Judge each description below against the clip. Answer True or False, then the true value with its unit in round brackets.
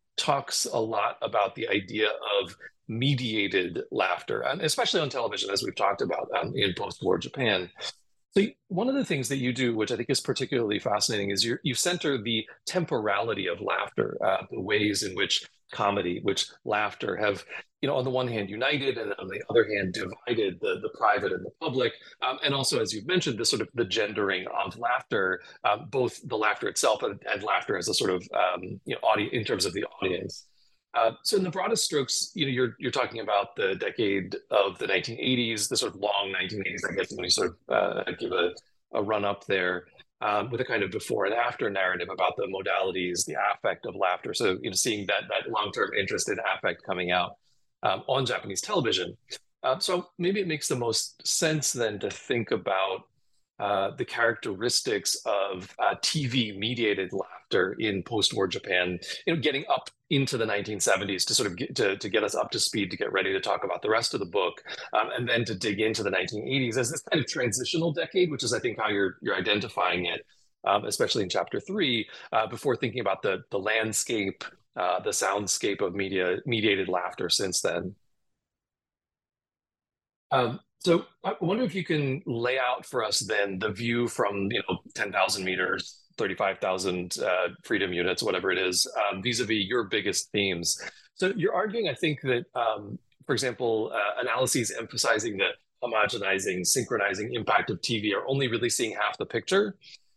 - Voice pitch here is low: True (120 Hz)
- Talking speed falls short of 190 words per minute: False (195 wpm)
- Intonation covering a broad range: True (8.8 semitones)